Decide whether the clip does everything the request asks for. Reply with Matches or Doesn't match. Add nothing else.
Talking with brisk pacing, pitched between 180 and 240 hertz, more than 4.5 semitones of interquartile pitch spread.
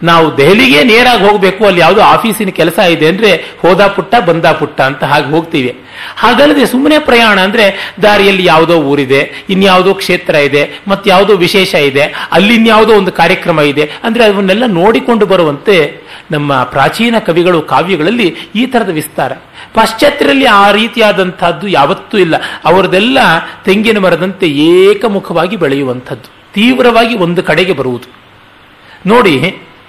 Matches